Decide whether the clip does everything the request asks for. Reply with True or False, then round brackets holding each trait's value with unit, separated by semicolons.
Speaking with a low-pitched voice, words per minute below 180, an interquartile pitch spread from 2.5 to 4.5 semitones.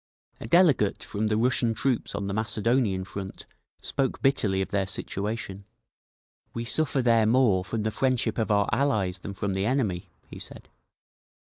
True (110 Hz; 160 wpm; 3.8 semitones)